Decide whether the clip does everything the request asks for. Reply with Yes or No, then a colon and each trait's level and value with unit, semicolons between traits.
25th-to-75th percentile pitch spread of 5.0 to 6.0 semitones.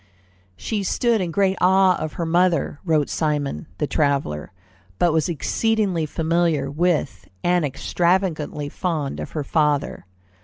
No: average, 3.6 semitones